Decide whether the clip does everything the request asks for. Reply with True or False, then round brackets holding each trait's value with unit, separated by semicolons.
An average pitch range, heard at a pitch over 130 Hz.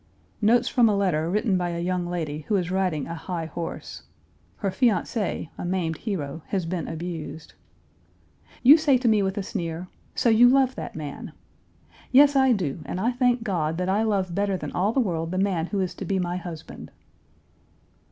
True (4.5 semitones; 185 Hz)